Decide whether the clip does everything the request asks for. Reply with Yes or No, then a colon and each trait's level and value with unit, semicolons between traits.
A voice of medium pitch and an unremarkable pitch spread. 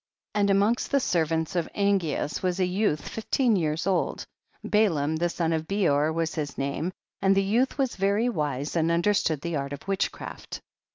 Yes: medium, 175 Hz; average, 4.2 semitones